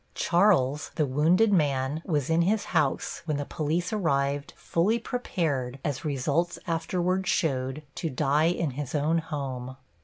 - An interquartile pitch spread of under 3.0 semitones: No, average, 3.8 semitones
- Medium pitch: Yes, medium, 155 Hz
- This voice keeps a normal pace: Yes, average, 145 wpm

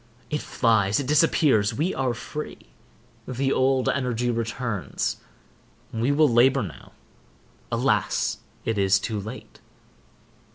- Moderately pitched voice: No, low, 125 Hz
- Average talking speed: No, slow, 100 wpm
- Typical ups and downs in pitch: Yes, average, 3.5 semitones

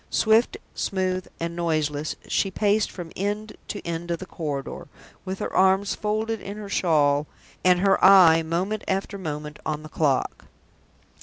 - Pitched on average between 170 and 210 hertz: Yes, medium, 185 Hz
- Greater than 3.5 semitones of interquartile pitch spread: Yes, average, 4.0 semitones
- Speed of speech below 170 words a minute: Yes, average, 155 wpm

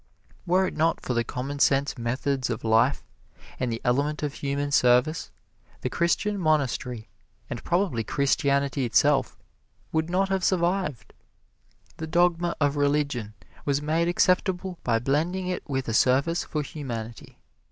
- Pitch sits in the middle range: Yes, medium, 145 Hz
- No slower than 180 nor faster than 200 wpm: No, average, 140 wpm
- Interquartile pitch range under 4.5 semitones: No, average, 5.1 semitones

